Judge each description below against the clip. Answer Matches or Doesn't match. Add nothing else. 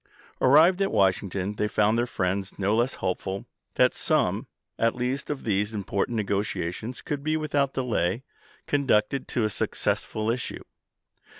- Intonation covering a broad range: Doesn't match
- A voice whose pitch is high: Doesn't match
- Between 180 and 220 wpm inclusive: Doesn't match